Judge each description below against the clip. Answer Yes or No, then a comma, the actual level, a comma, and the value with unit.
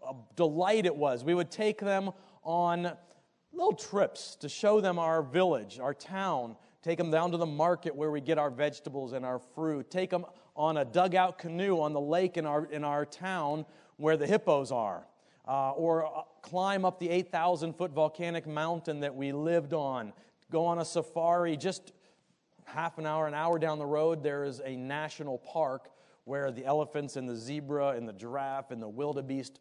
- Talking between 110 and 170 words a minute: No, average, 185 wpm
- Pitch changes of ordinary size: Yes, average, 3.2 semitones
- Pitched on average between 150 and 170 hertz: Yes, medium, 160 Hz